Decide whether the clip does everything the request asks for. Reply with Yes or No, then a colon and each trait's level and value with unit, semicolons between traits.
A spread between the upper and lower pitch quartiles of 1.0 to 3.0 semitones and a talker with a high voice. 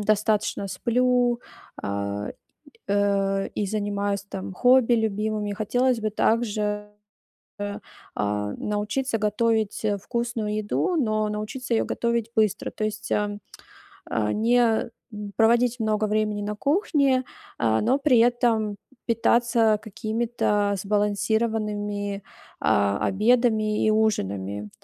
Yes: narrow, 2.5 semitones; high, 215 Hz